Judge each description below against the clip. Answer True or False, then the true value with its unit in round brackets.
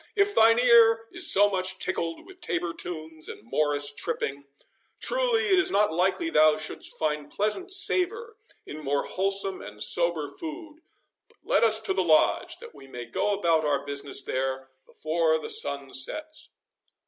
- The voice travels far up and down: True (8.9 semitones)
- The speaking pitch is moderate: True (175 Hz)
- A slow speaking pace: False (165 wpm)